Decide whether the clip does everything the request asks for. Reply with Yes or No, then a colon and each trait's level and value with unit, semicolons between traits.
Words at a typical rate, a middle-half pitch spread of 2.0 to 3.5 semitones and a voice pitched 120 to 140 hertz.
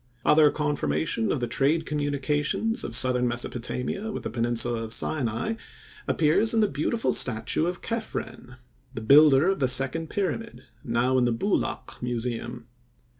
No: average, 145 wpm; average, 4.8 semitones; low, 135 Hz